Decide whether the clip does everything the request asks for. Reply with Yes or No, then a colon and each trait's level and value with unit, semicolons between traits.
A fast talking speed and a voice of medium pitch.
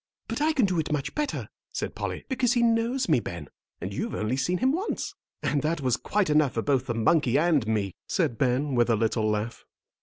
Yes: fast, 220 wpm; medium, 145 Hz